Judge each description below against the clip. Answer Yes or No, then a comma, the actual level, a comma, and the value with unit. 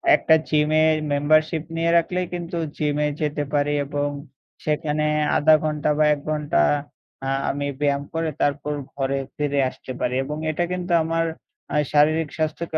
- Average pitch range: No, narrow, 1.6 semitones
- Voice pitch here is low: No, medium, 150 Hz